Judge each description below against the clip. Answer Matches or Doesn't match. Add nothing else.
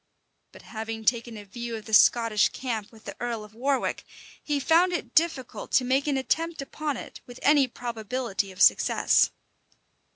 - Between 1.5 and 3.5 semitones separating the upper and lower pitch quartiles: Doesn't match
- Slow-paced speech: Doesn't match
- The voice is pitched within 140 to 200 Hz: Doesn't match